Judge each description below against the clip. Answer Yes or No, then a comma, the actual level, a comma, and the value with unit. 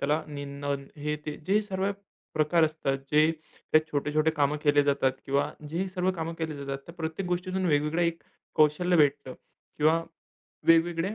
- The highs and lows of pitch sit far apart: No, average, 2.8 semitones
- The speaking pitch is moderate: Yes, medium, 155 Hz